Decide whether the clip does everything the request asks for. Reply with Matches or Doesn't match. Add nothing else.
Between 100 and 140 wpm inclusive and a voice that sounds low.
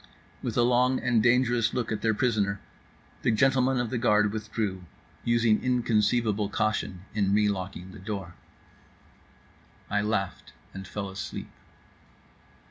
Matches